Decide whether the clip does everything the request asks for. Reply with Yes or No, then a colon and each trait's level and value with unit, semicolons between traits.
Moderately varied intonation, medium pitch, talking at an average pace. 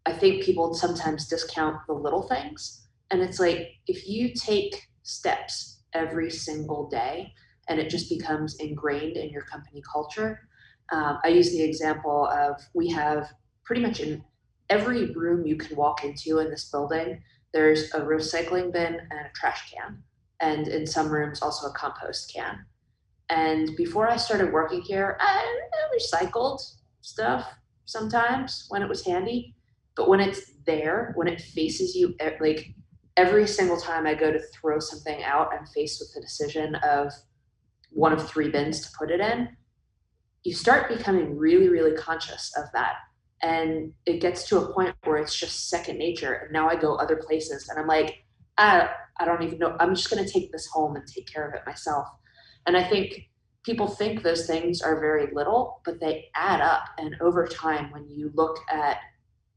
Yes: average, 3.0 semitones; medium, 160 Hz; average, 175 wpm